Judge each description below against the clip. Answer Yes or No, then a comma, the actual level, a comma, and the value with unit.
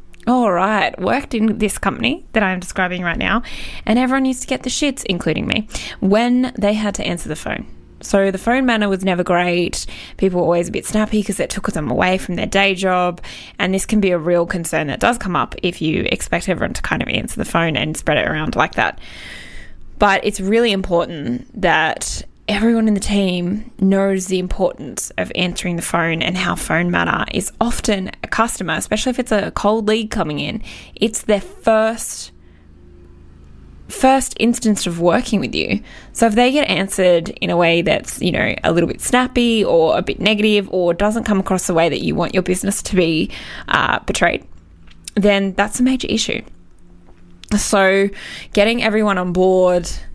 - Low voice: No, high, 195 Hz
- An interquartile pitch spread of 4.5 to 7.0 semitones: No, average, 3.9 semitones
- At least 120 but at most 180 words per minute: No, average, 195 wpm